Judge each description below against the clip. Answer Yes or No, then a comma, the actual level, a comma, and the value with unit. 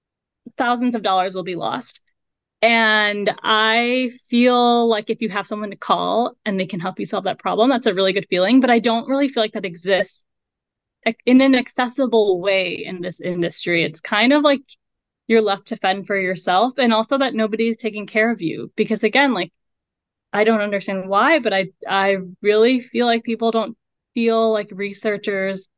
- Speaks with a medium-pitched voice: No, high, 220 Hz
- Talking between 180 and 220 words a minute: Yes, average, 185 wpm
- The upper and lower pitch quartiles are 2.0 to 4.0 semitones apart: Yes, average, 3.4 semitones